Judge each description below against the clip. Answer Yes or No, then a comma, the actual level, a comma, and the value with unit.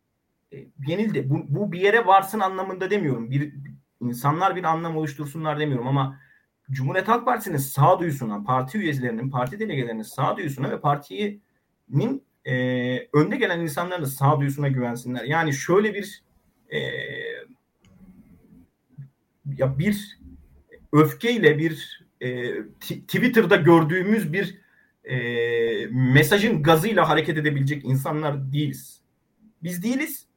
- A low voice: No, medium, 150 Hz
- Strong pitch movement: Yes, wide, 6.3 semitones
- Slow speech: No, average, 115 wpm